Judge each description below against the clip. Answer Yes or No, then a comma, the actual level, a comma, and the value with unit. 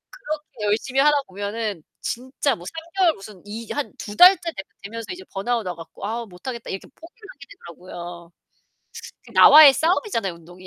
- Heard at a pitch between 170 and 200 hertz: No, high, 225 Hz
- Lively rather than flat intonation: Yes, wide, 7.4 semitones